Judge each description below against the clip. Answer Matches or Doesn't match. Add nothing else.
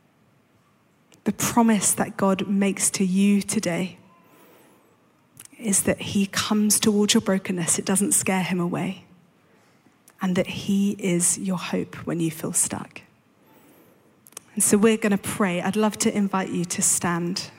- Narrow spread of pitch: Matches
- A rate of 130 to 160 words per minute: Matches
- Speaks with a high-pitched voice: Matches